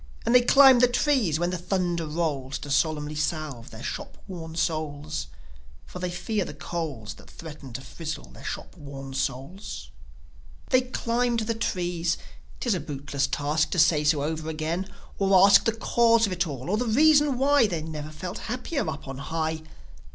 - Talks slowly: No, average, 180 wpm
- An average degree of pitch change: No, wide, 6.3 semitones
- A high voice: No, medium, 165 Hz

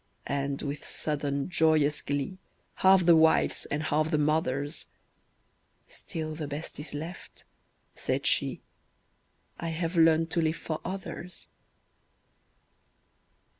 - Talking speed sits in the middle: No, slow, 115 wpm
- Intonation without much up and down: Yes, narrow, 2.2 semitones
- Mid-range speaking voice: Yes, medium, 155 Hz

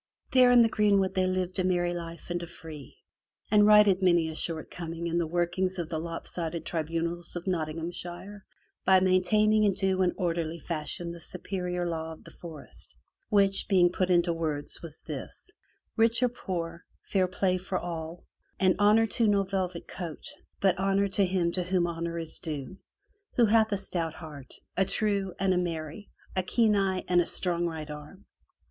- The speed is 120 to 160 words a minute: No, average, 180 wpm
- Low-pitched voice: No, medium, 180 Hz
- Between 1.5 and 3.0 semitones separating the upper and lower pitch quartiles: Yes, narrow, 2.6 semitones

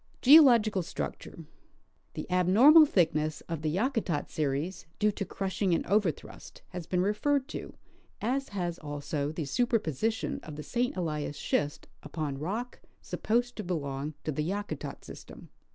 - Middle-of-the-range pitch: Yes, medium, 180 Hz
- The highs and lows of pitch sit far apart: Yes, wide, 6.4 semitones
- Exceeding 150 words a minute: No, average, 145 wpm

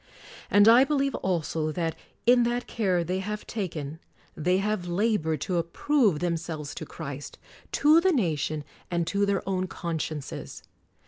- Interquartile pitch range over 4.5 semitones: Yes, average, 5.0 semitones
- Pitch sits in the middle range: Yes, medium, 180 Hz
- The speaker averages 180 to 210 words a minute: No, average, 150 wpm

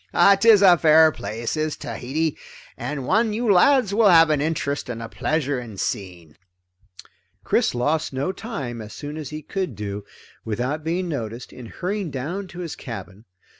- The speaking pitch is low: No, medium, 150 Hz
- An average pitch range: No, wide, 6.7 semitones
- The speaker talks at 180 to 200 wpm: No, average, 170 wpm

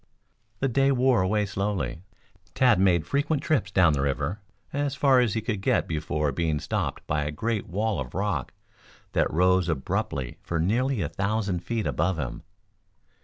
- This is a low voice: Yes, very low, 95 Hz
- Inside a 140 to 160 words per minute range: No, average, 170 wpm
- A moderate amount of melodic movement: No, wide, 7.0 semitones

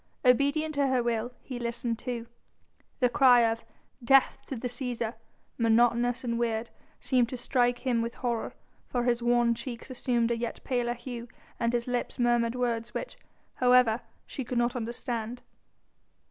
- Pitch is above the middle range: Yes, high, 240 Hz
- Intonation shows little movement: Yes, narrow, 1.2 semitones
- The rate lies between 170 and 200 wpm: No, average, 160 wpm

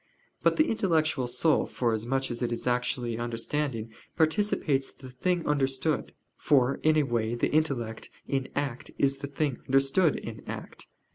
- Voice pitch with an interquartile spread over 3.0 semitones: Yes, average, 3.9 semitones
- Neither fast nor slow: Yes, average, 150 wpm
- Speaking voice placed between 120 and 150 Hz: Yes, low, 135 Hz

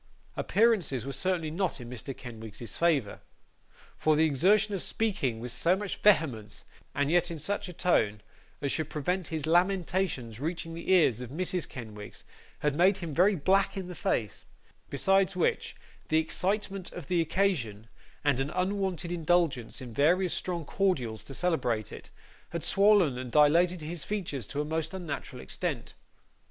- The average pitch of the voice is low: No, medium, 165 Hz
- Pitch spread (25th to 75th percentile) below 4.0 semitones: No, wide, 5.4 semitones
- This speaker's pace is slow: No, average, 160 wpm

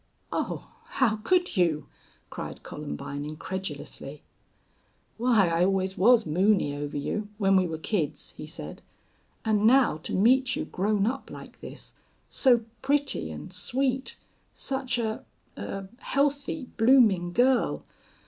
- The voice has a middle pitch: No, high, 210 Hz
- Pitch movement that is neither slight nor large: No, wide, 6.5 semitones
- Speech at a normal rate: No, slow, 130 wpm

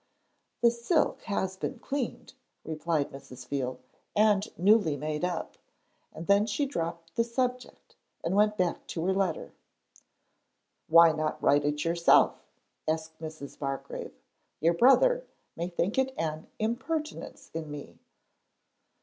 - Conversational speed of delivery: No, slow, 130 wpm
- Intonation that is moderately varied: No, wide, 6.2 semitones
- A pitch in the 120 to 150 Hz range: No, medium, 170 Hz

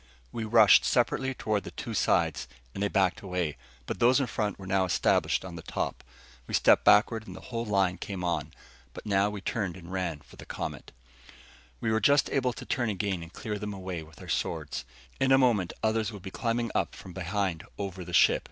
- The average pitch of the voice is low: Yes, low, 100 Hz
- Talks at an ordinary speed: No, fast, 215 wpm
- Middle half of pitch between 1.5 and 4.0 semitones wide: Yes, average, 3.5 semitones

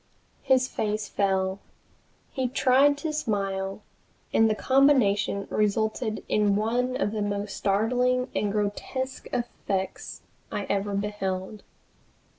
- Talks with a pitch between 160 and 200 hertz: No, high, 210 Hz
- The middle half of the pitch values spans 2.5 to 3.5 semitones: No, average, 4.0 semitones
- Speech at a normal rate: No, slow, 110 wpm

